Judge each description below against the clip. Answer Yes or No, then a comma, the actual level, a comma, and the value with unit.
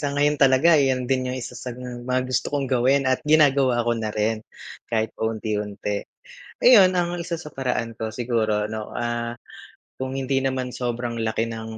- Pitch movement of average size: Yes, average, 3.0 semitones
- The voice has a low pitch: Yes, low, 125 Hz